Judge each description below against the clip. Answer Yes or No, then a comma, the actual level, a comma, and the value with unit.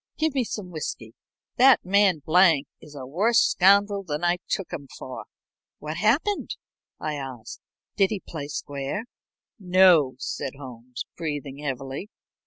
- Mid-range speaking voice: Yes, medium, 160 Hz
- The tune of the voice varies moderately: No, wide, 6.2 semitones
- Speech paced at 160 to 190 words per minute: No, average, 140 wpm